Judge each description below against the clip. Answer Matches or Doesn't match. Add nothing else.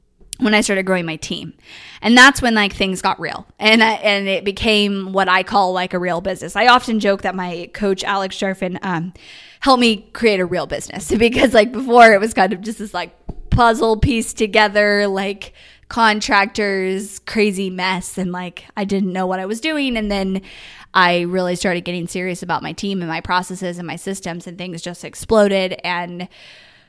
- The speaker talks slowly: Doesn't match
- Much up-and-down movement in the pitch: Doesn't match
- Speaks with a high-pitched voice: Matches